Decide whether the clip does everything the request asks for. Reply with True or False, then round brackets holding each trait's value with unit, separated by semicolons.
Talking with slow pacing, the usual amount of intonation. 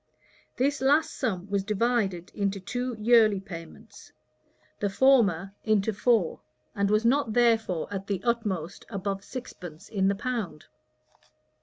True (130 wpm; 3.6 semitones)